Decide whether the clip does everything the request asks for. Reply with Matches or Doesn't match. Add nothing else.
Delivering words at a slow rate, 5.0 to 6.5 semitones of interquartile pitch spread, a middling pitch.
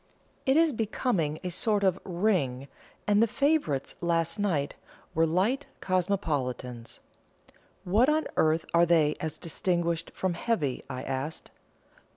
Matches